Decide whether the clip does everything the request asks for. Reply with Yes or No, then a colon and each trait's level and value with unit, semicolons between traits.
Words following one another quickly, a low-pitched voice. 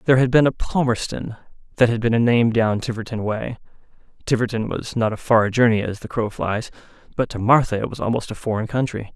Yes: fast, 210 wpm; low, 115 Hz